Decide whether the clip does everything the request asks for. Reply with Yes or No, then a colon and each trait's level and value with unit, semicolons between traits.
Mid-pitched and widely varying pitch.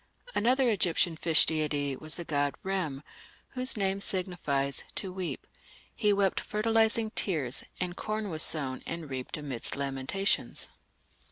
Yes: medium, 175 Hz; wide, 5.9 semitones